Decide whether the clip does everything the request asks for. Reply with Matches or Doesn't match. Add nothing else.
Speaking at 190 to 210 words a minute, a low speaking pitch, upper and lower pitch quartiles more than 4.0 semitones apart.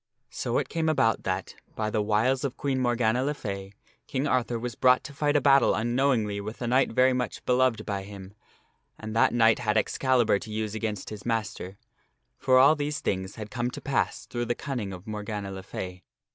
Doesn't match